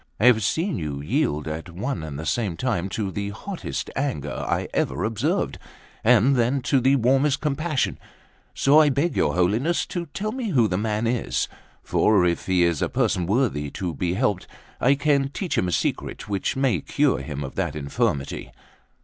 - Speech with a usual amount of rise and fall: No, wide, 7.9 semitones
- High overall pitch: No, low, 110 Hz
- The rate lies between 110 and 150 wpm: No, average, 185 wpm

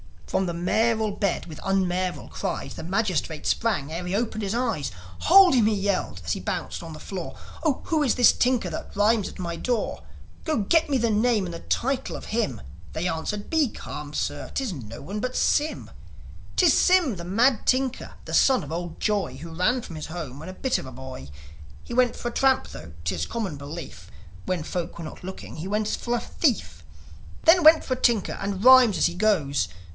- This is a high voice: Yes, high, 200 Hz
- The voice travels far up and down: Yes, wide, 6.6 semitones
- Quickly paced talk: Yes, fast, 210 wpm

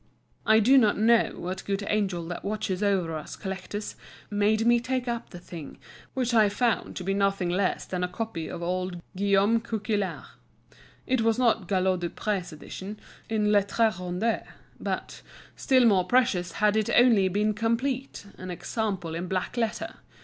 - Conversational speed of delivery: Yes, average, 165 wpm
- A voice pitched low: No, high, 205 Hz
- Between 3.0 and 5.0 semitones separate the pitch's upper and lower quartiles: Yes, average, 3.5 semitones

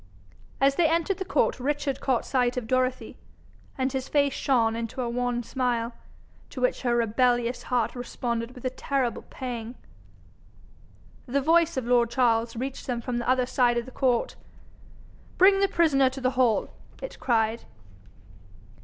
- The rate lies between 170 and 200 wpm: No, average, 160 wpm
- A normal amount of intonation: No, narrow, 2.2 semitones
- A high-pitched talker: Yes, very high, 250 Hz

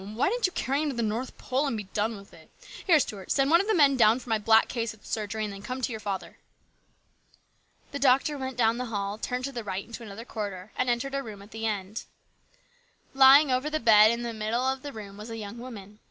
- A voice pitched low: No, high, 230 Hz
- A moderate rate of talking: No, fast, 255 wpm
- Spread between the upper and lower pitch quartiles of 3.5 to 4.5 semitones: Yes, average, 3.8 semitones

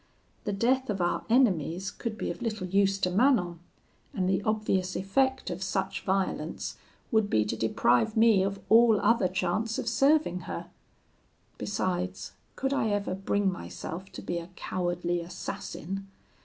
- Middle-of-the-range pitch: No, high, 195 Hz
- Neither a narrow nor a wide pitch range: Yes, average, 3.7 semitones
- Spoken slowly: No, average, 155 wpm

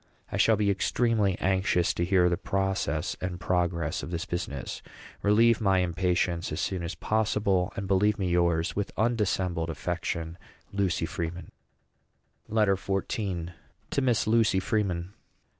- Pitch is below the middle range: Yes, very low, 95 Hz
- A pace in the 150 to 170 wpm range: No, average, 140 wpm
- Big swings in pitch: No, average, 2.9 semitones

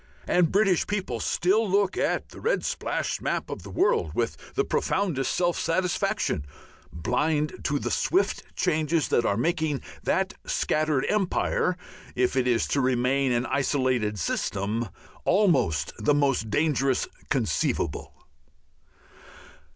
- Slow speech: Yes, slow, 130 wpm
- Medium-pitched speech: Yes, medium, 150 Hz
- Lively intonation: Yes, wide, 6.4 semitones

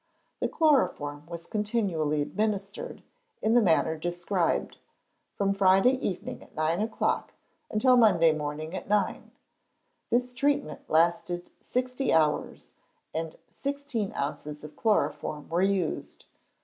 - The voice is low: No, high, 190 Hz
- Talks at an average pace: No, slow, 115 wpm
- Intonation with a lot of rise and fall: Yes, wide, 5.9 semitones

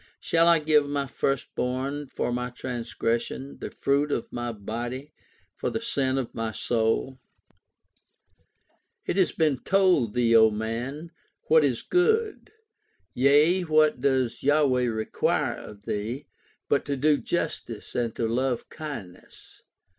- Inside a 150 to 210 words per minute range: No, slow, 135 wpm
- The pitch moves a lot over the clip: No, average, 4.3 semitones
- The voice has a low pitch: Yes, low, 130 Hz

